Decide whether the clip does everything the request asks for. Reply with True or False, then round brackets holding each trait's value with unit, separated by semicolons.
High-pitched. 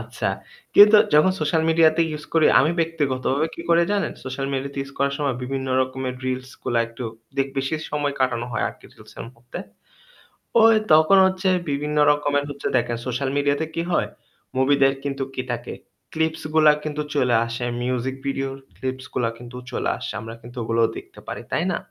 False (140 Hz)